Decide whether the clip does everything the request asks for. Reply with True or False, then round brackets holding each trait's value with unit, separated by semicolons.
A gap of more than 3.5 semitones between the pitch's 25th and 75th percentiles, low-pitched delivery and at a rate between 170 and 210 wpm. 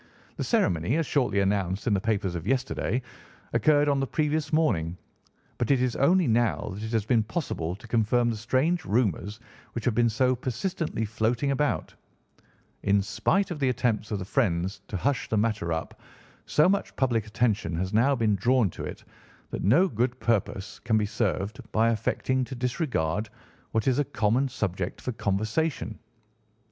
True (4.3 semitones; 115 Hz; 175 wpm)